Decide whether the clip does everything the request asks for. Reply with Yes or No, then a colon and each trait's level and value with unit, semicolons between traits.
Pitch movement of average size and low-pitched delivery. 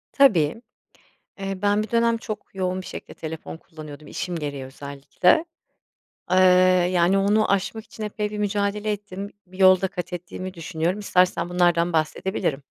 No: average, 3.5 semitones; medium, 185 Hz